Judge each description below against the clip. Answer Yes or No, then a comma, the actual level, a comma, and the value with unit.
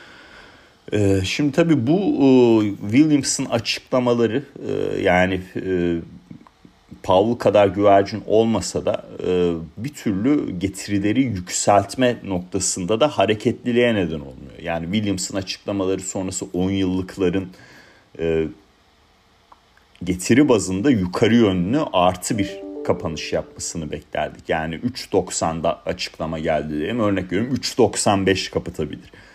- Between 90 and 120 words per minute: Yes, average, 100 wpm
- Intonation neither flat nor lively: Yes, average, 3.8 semitones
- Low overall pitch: Yes, low, 100 Hz